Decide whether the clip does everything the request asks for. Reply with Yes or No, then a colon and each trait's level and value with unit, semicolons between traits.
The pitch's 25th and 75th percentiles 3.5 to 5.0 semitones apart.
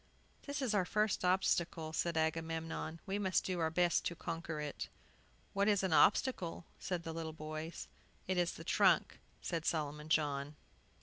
No: average, 2.8 semitones